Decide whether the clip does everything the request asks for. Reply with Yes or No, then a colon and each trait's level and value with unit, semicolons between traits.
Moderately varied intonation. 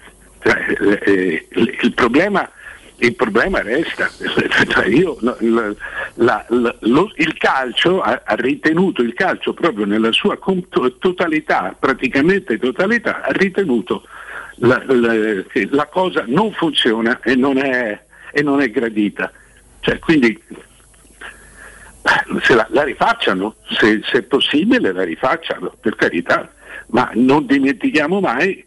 No: wide, 7.6 semitones